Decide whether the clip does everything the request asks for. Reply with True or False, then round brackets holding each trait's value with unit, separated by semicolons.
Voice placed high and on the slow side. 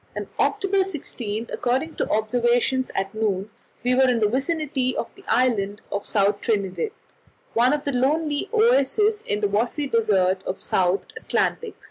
False (245 Hz; 165 wpm)